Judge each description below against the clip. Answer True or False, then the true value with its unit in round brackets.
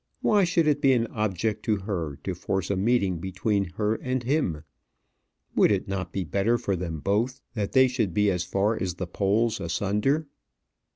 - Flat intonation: False (4.1 semitones)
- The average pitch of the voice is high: False (100 Hz)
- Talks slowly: False (180 wpm)